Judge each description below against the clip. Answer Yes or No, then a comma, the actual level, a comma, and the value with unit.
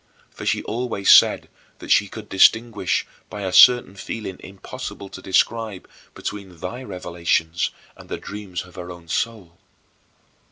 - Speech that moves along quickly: No, average, 145 wpm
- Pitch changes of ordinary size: Yes, average, 3.4 semitones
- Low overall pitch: Yes, low, 100 Hz